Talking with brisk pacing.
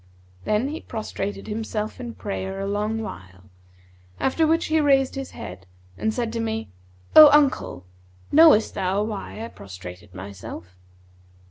No: average, 140 wpm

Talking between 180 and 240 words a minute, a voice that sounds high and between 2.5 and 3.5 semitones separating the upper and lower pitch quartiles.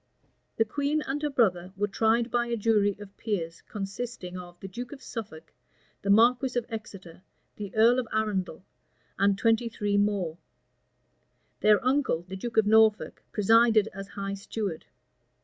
No: average, 155 wpm; high, 215 Hz; average, 3.2 semitones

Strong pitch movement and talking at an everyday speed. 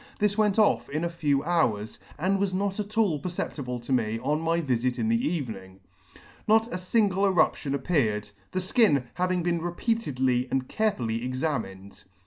Yes: wide, 7.4 semitones; average, 165 wpm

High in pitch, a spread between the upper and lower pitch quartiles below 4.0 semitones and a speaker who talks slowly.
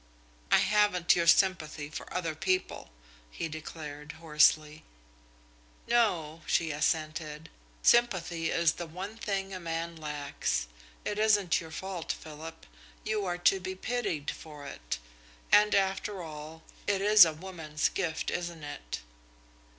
No: medium, 165 Hz; average, 3.6 semitones; slow, 130 wpm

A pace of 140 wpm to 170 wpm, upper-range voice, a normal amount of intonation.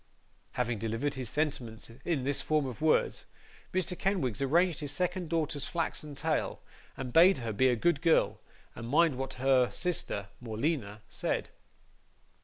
No: average, 150 wpm; medium, 140 Hz; average, 5.0 semitones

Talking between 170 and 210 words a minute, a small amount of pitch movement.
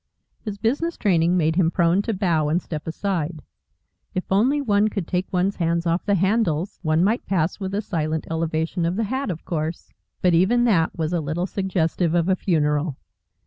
No: average, 190 wpm; average, 3.6 semitones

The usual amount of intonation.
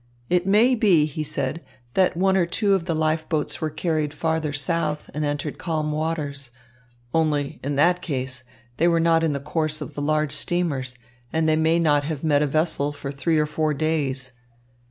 No: narrow, 2.3 semitones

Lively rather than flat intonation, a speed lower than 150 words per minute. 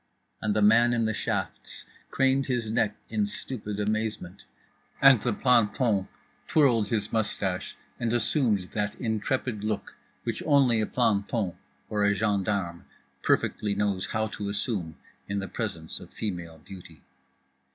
No: average, 2.8 semitones; average, 140 wpm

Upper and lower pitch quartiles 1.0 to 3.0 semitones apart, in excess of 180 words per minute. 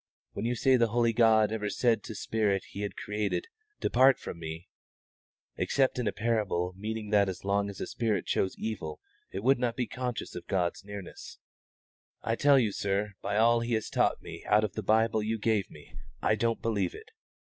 Yes: narrow, 2.5 semitones; average, 200 wpm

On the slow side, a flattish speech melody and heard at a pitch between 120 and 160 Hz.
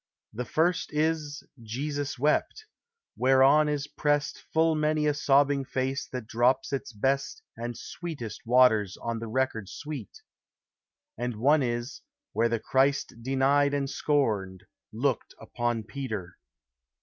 No: slow, 125 wpm; average, 3.8 semitones; low, 135 Hz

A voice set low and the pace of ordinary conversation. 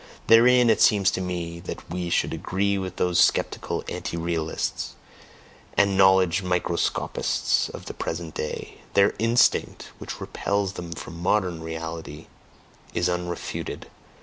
No: very low, 90 Hz; slow, 130 wpm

